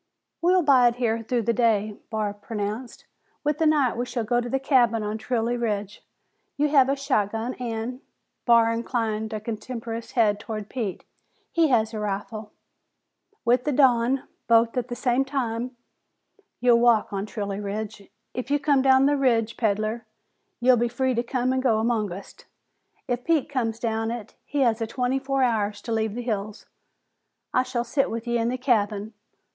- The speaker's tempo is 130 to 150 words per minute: No, average, 180 wpm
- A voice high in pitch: Yes, high, 235 Hz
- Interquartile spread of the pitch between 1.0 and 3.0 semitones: Yes, narrow, 2.6 semitones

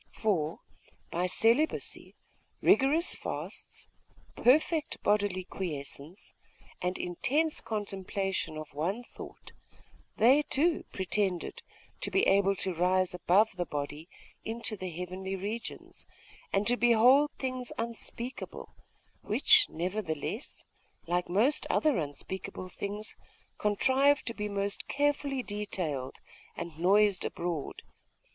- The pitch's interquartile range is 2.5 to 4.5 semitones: No, average, 5.3 semitones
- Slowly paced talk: Yes, slow, 105 wpm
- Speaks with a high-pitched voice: Yes, high, 200 Hz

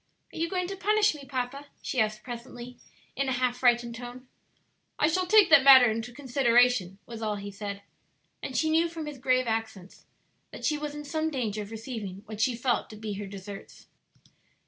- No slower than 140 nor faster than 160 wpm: No, average, 195 wpm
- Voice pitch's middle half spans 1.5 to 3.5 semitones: No, average, 4.8 semitones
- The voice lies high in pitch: Yes, high, 245 Hz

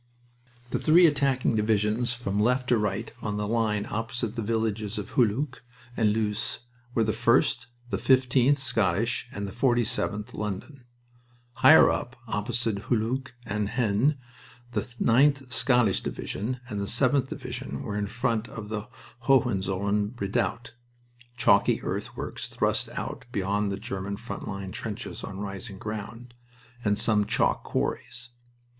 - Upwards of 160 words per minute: No, average, 140 wpm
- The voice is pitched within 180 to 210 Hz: No, low, 110 Hz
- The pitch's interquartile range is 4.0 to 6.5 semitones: No, average, 3.1 semitones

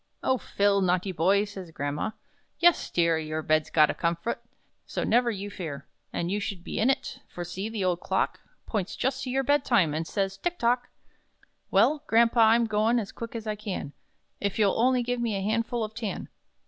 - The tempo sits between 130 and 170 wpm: No, average, 200 wpm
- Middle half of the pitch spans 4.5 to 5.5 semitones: Yes, average, 4.9 semitones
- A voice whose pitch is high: Yes, high, 210 Hz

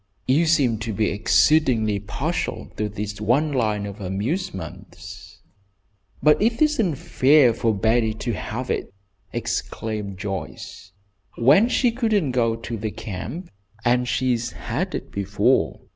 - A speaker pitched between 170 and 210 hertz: No, low, 115 Hz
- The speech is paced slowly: Yes, slow, 130 wpm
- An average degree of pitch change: No, wide, 6.1 semitones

